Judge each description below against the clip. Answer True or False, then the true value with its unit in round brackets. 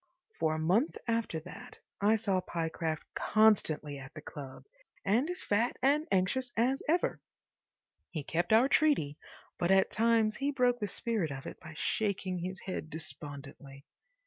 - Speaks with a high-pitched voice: True (195 Hz)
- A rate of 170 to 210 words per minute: False (155 wpm)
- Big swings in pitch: True (6.7 semitones)